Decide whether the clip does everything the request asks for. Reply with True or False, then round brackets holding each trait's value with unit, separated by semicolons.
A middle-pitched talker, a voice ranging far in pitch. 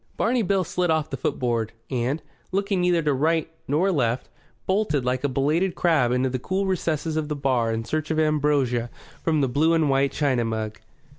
False (150 Hz; 4.6 semitones)